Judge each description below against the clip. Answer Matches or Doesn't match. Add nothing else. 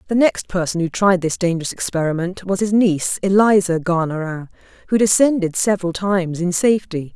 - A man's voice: Doesn't match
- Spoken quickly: Doesn't match